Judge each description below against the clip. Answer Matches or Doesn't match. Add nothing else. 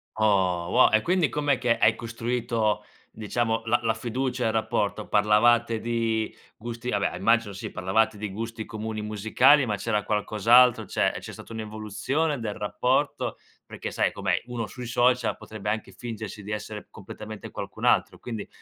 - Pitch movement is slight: Matches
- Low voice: Matches